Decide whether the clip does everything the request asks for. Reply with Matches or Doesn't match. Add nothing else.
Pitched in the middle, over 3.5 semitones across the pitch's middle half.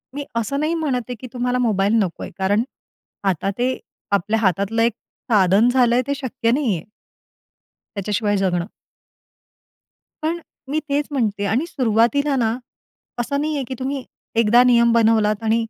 Doesn't match